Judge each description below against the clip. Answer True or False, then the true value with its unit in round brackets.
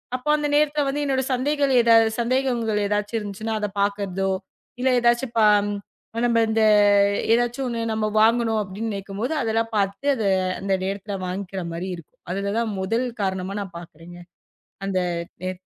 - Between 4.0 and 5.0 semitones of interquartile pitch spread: False (3.6 semitones)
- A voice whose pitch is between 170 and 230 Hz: True (220 Hz)